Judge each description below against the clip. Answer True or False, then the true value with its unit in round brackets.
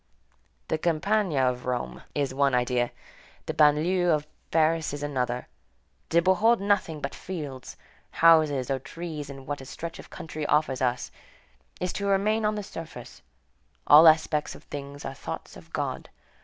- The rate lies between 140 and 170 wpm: True (155 wpm)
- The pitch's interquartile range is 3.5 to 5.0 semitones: True (4.0 semitones)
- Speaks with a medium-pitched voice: True (150 Hz)